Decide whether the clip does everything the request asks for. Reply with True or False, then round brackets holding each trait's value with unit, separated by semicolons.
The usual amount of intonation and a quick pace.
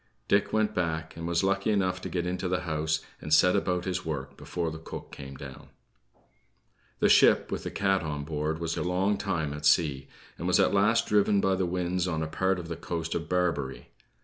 True (3.1 semitones; 215 wpm)